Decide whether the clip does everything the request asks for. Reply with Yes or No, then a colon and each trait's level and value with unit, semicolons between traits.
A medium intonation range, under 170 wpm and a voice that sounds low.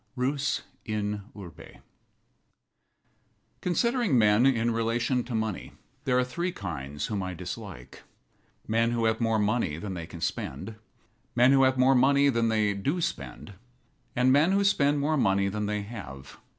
Yes: average, 4.6 semitones; average, 155 wpm; low, 115 Hz